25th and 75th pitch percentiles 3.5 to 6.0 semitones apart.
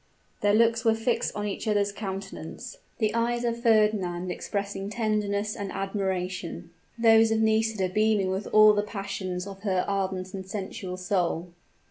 No: narrow, 2.5 semitones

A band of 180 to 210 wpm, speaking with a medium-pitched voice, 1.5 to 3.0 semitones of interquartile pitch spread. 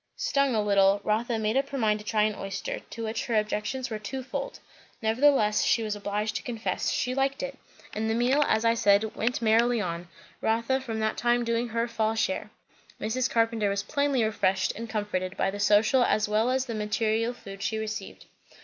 No: average, 200 wpm; high, 220 Hz; narrow, 2.4 semitones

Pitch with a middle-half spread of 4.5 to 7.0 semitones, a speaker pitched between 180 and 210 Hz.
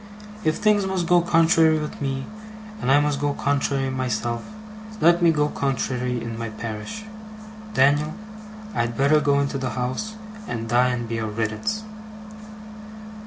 No: average, 4.9 semitones; medium, 140 Hz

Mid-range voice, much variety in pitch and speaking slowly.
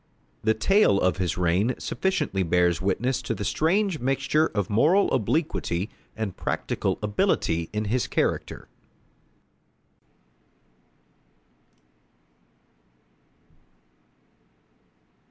No: low, 110 Hz; wide, 6.7 semitones; slow, 80 wpm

